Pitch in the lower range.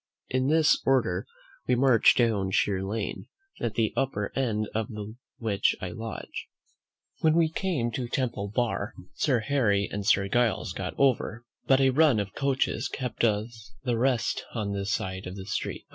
Yes: low, 115 Hz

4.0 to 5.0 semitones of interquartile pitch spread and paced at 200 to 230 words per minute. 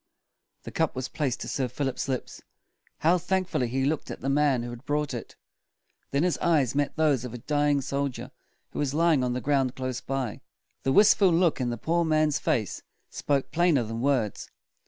No: average, 3.4 semitones; fast, 205 wpm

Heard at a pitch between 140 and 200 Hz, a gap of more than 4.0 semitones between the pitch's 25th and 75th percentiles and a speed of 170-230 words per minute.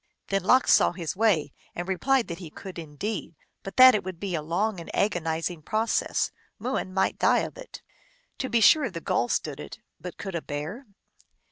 Yes: high, 190 Hz; average, 4.9 semitones; average, 195 wpm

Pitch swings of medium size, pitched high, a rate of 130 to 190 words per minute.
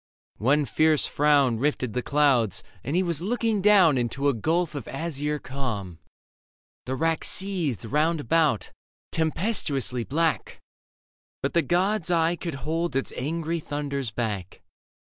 No: average, 4.3 semitones; medium, 150 Hz; slow, 135 wpm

